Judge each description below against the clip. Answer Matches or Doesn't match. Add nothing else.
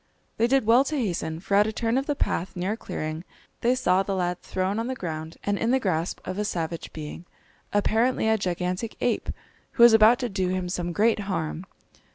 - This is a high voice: Matches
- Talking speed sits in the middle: Doesn't match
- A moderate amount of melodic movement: Matches